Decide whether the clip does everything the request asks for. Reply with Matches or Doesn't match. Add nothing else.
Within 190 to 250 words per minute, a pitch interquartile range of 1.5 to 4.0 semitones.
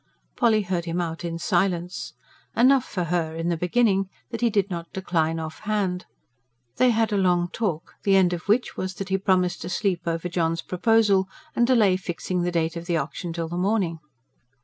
Matches